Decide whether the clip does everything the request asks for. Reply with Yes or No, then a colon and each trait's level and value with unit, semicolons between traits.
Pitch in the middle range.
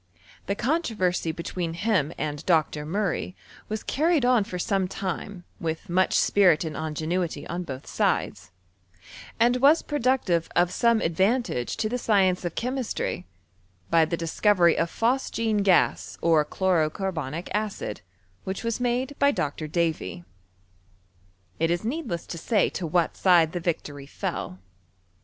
Yes: medium, 180 Hz